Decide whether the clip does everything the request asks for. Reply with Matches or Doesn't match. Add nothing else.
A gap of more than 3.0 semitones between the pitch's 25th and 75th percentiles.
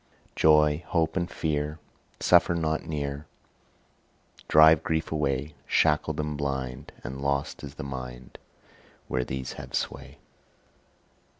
Doesn't match